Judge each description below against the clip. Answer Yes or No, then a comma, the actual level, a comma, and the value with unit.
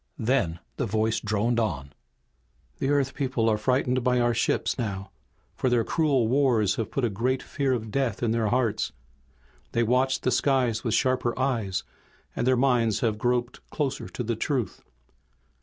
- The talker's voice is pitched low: Yes, low, 120 Hz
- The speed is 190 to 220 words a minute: No, average, 170 wpm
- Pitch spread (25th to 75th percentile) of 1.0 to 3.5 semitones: Yes, average, 2.8 semitones